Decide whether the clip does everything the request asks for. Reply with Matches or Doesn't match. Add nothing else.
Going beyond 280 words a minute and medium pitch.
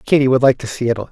Doesn't match